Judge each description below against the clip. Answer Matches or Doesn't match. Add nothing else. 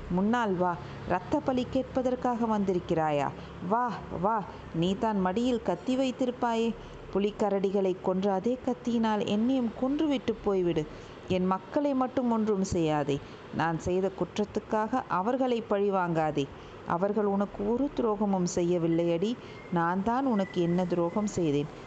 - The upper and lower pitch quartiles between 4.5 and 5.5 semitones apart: Matches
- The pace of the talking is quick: Doesn't match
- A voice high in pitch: Matches